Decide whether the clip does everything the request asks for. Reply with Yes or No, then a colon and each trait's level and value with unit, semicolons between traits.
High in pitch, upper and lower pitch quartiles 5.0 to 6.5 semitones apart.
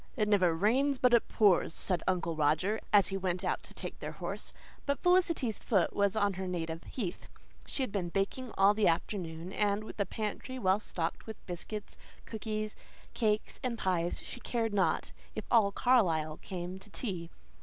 No: high, 200 Hz; average, 3.7 semitones